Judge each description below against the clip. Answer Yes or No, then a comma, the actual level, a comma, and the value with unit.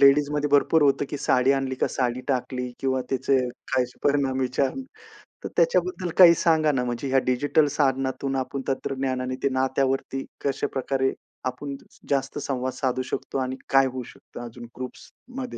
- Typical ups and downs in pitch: No, narrow, 1.6 semitones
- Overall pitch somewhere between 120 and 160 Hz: Yes, low, 135 Hz